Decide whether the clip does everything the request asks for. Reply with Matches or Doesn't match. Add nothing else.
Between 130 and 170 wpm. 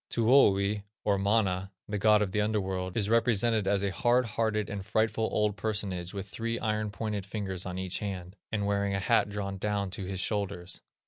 Doesn't match